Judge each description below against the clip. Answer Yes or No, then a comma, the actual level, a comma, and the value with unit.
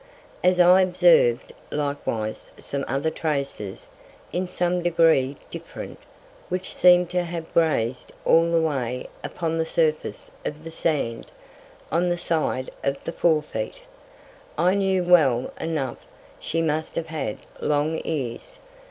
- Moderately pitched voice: Yes, medium, 160 Hz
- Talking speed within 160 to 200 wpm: No, slow, 135 wpm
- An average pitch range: Yes, average, 3.8 semitones